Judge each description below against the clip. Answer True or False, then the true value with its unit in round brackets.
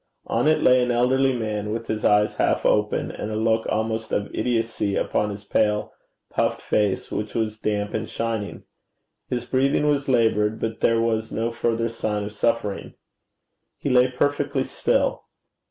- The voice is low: True (115 Hz)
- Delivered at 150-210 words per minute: True (165 wpm)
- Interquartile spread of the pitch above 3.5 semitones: False (2.6 semitones)